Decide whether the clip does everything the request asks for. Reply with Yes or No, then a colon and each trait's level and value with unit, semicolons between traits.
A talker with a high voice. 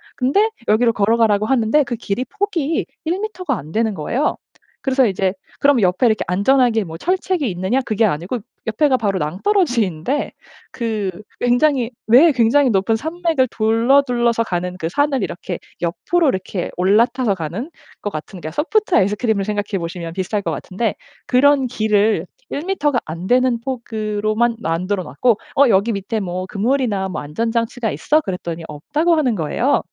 Yes: high, 225 Hz